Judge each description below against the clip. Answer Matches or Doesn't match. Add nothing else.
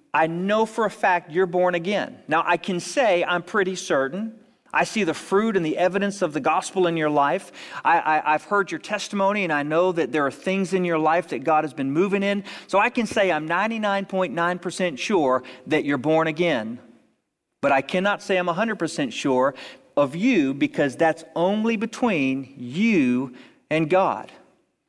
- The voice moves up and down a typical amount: Matches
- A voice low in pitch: Doesn't match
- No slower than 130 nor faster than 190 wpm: Matches